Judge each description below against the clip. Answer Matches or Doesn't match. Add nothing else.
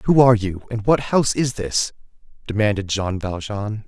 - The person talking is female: Doesn't match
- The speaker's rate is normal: Matches